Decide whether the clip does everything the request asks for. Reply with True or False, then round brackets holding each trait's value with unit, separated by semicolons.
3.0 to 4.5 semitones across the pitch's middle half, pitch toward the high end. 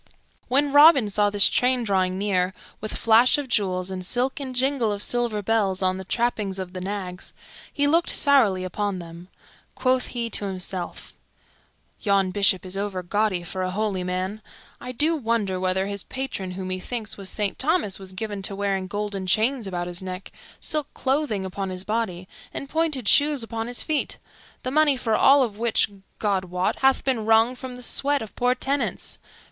False (5.0 semitones; 210 Hz)